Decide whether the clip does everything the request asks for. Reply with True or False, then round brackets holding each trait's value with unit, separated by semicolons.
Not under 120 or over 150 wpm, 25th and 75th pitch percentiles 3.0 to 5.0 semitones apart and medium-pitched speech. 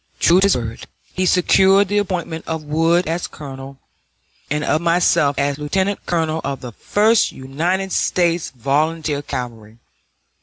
True (145 wpm; 4.4 semitones; 160 Hz)